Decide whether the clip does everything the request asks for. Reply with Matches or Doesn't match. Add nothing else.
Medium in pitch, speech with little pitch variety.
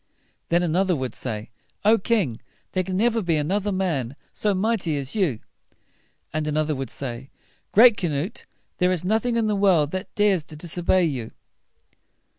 Doesn't match